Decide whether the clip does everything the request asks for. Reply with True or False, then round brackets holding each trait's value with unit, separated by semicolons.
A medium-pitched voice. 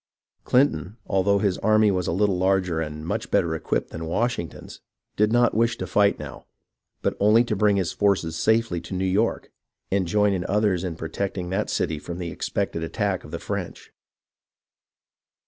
False (95 Hz)